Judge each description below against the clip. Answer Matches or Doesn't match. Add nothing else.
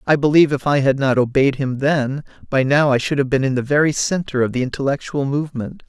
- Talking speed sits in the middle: Doesn't match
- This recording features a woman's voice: Doesn't match